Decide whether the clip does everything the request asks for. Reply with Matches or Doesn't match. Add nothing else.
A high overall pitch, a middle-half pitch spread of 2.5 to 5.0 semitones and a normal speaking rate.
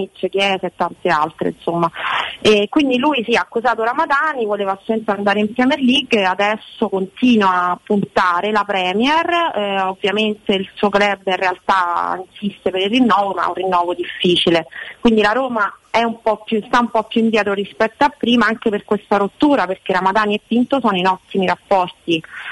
Doesn't match